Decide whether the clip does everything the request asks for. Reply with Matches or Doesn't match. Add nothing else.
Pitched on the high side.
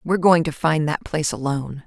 Doesn't match